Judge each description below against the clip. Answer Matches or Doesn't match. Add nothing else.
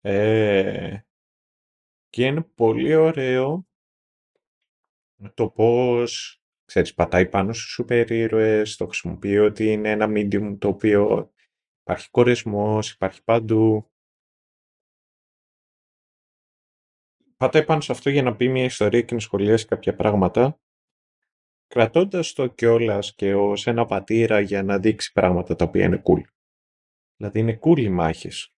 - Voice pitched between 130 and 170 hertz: Doesn't match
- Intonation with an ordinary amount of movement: Matches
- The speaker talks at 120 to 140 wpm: Matches